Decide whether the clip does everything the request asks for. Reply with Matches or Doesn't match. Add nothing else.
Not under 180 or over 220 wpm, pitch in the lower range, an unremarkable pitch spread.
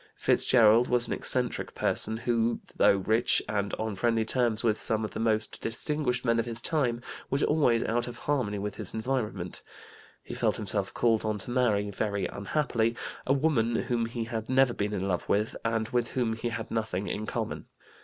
Doesn't match